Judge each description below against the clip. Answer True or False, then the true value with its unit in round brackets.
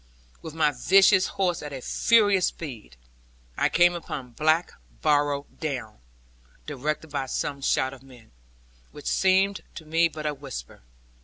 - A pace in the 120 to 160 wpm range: True (145 wpm)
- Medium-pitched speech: True (150 Hz)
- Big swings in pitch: False (4.3 semitones)